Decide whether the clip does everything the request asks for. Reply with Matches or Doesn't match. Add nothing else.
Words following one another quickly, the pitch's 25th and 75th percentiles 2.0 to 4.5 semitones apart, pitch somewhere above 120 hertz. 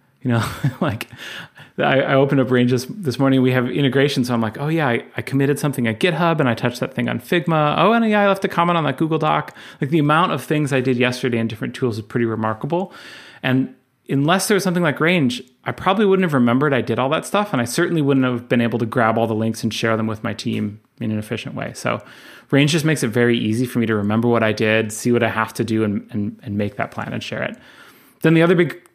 Doesn't match